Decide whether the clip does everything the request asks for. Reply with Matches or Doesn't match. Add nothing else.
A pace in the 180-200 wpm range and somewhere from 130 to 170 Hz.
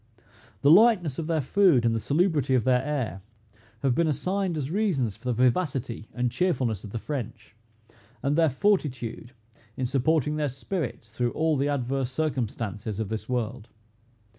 Doesn't match